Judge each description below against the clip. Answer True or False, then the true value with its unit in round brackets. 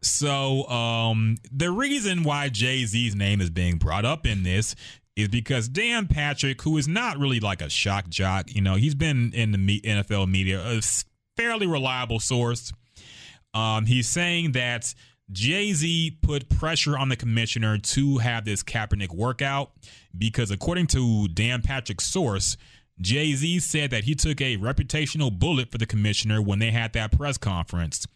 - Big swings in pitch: False (5.0 semitones)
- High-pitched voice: False (115 Hz)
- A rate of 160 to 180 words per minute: True (165 wpm)